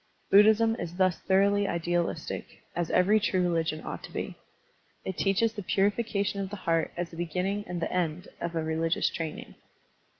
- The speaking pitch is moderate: Yes, medium, 180 Hz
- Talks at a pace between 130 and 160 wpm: No, average, 170 wpm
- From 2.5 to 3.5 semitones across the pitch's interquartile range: Yes, average, 3.2 semitones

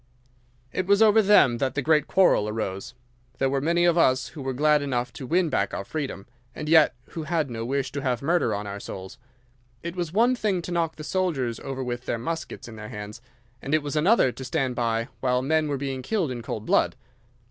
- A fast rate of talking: Yes, fast, 225 wpm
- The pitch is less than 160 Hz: Yes, medium, 140 Hz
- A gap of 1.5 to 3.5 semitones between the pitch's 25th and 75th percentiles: No, average, 5.3 semitones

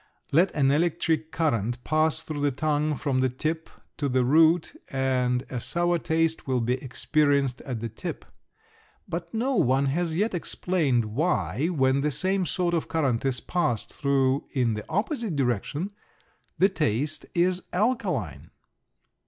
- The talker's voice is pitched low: No, medium, 150 Hz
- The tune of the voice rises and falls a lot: No, average, 4.7 semitones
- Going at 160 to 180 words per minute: No, average, 150 wpm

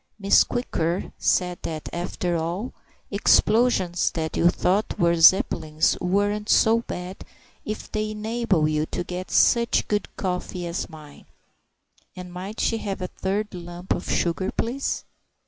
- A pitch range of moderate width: Yes, average, 3.5 semitones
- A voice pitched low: No, medium, 185 Hz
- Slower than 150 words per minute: Yes, average, 140 wpm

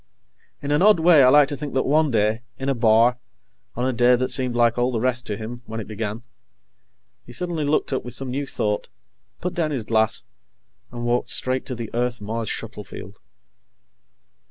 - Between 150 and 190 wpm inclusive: No, fast, 205 wpm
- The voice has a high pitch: No, low, 125 Hz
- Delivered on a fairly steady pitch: No, average, 3.2 semitones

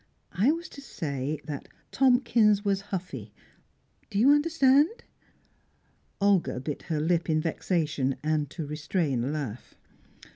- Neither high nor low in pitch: Yes, medium, 170 Hz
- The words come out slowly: Yes, slow, 125 wpm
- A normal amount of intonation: No, wide, 7.4 semitones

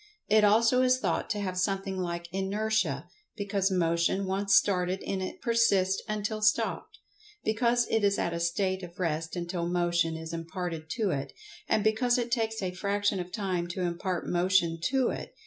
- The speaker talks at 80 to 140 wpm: No, average, 180 wpm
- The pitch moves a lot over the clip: No, average, 3.5 semitones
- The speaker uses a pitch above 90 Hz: Yes, high, 190 Hz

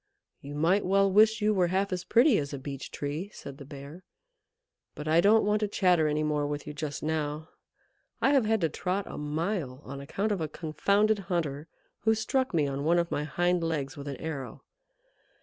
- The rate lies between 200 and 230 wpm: Yes, fast, 205 wpm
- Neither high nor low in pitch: Yes, medium, 165 Hz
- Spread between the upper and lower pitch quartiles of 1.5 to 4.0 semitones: No, average, 5.3 semitones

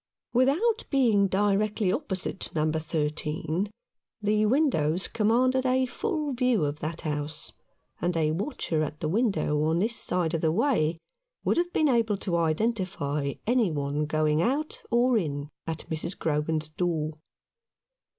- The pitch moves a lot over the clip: Yes, wide, 7.4 semitones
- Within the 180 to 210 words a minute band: No, average, 140 wpm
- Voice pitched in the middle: Yes, medium, 180 Hz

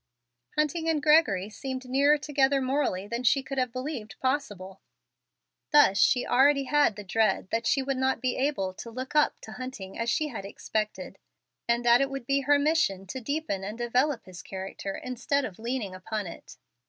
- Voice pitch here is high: Yes, very high, 255 Hz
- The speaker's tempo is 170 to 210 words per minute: Yes, average, 185 wpm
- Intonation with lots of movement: No, average, 4.8 semitones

